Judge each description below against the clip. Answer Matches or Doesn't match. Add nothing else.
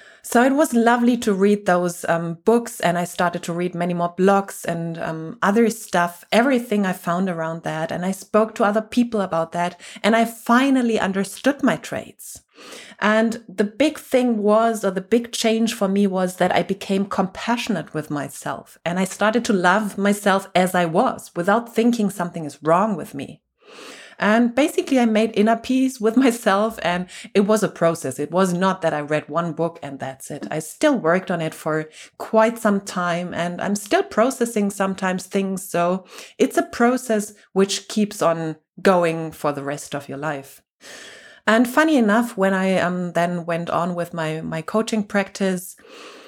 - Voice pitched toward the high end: Matches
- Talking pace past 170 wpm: Matches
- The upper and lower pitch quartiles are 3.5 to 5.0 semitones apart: Matches